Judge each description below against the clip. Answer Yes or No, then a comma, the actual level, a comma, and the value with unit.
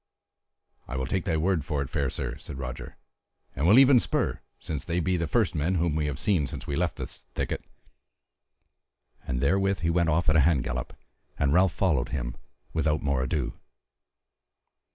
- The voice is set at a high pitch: No, very low, 80 Hz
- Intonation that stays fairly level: No, average, 4.2 semitones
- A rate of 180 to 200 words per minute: Yes, average, 185 wpm